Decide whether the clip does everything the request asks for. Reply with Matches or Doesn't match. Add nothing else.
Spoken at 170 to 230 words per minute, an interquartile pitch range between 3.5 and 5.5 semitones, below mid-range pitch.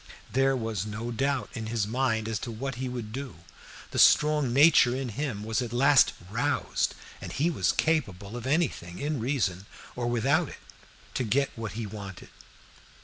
Matches